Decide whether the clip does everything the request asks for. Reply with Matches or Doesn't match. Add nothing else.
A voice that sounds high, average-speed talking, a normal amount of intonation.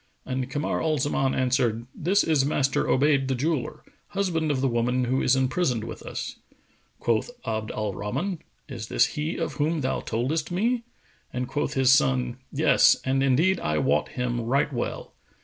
Doesn't match